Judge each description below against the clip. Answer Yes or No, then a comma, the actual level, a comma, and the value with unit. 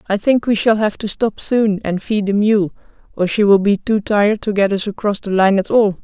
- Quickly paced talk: Yes, fast, 260 wpm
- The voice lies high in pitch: Yes, high, 205 Hz